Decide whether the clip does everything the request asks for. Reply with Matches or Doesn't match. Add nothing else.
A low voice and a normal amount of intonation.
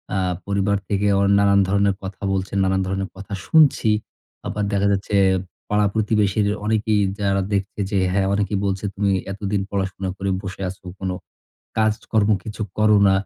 Doesn't match